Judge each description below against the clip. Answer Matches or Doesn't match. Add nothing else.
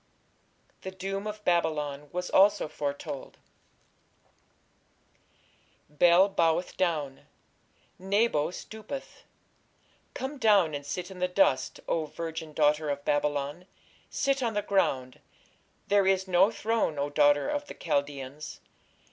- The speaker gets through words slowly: Matches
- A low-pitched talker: Doesn't match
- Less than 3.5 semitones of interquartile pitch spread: Doesn't match